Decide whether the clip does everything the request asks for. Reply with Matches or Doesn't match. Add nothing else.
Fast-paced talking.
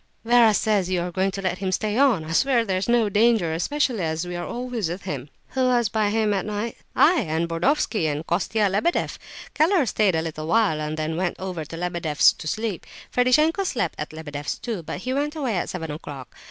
Matches